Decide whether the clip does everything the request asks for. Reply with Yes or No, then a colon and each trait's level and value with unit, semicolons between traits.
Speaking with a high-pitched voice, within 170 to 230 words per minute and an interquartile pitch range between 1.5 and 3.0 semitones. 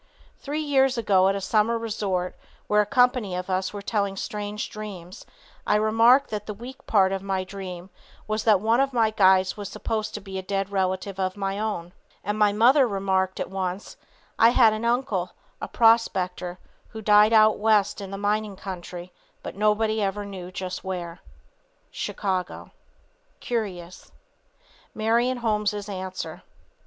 No: high, 205 Hz; average, 160 wpm; average, 2.7 semitones